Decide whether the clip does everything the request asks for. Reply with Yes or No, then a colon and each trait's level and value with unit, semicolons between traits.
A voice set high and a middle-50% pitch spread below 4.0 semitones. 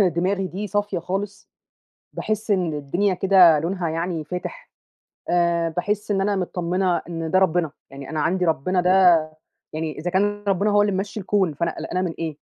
No: medium, 180 Hz; average, 2.9 semitones